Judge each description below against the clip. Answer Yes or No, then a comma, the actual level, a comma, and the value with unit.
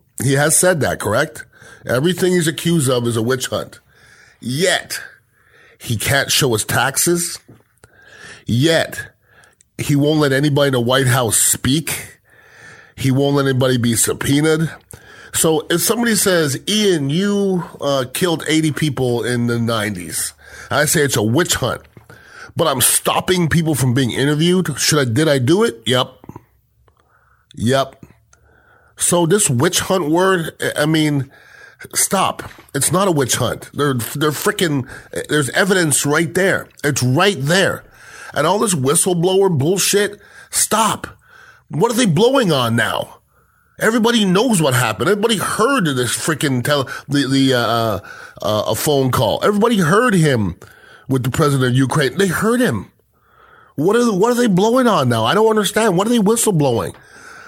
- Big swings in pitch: Yes, wide, 6.1 semitones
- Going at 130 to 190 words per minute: Yes, average, 155 wpm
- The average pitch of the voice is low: No, medium, 150 Hz